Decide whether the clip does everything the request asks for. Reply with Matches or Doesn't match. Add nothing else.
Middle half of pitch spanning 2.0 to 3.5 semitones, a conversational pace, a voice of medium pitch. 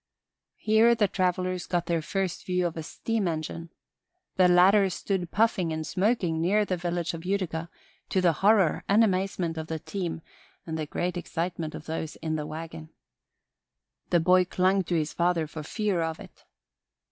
Matches